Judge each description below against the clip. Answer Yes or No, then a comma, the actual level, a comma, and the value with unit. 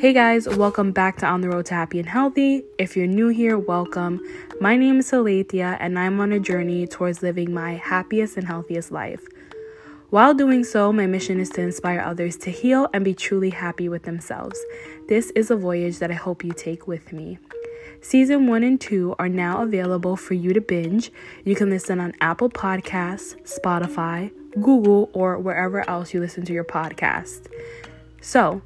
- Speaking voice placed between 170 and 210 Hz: Yes, medium, 185 Hz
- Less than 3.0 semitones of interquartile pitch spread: No, average, 4.1 semitones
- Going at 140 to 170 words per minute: No, average, 185 wpm